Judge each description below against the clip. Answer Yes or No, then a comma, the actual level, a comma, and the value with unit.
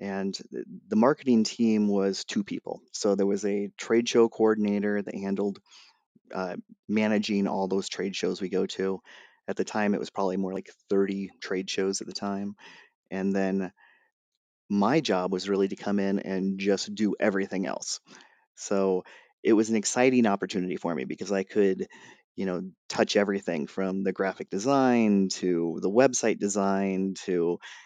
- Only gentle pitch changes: Yes, narrow, 1.8 semitones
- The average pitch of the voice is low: Yes, low, 100 Hz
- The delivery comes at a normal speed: Yes, average, 165 wpm